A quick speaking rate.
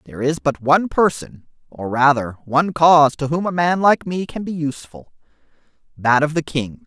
No: average, 185 wpm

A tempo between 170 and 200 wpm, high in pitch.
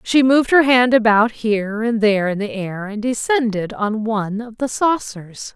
Yes: average, 195 wpm; high, 225 Hz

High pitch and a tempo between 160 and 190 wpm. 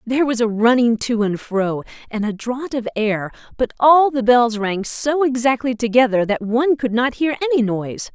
No: high, 240 Hz; average, 200 wpm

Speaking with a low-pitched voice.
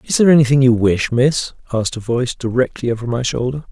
Yes: low, 125 Hz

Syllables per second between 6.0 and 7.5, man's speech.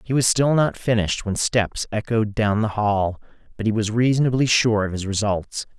No: 5.0 syllables/s; male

